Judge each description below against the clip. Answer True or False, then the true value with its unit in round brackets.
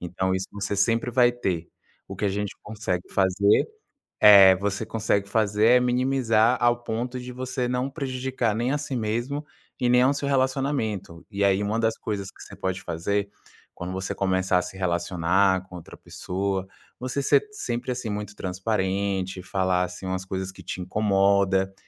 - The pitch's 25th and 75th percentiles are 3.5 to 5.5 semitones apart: True (4.4 semitones)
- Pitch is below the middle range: True (100 Hz)